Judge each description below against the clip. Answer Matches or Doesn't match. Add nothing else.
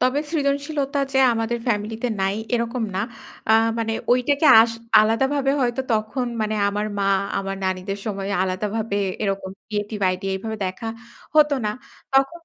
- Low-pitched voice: Doesn't match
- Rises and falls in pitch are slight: Doesn't match